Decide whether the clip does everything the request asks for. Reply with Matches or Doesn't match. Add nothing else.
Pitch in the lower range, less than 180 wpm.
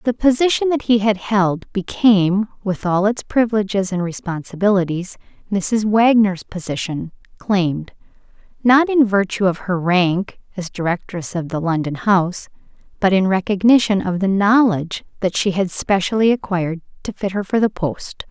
Doesn't match